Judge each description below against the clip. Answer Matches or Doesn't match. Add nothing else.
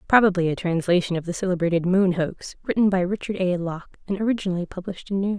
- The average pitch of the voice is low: Doesn't match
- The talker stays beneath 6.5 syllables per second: Doesn't match